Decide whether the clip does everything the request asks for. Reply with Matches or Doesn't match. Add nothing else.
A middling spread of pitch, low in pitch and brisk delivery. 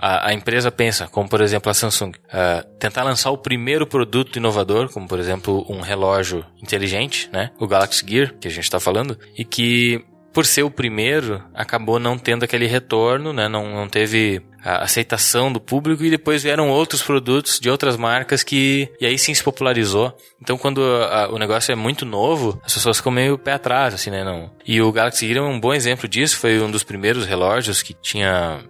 Matches